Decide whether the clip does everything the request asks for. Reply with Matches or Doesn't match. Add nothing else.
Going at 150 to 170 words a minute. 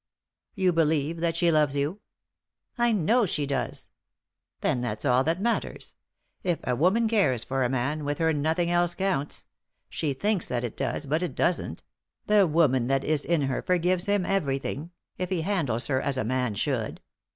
Doesn't match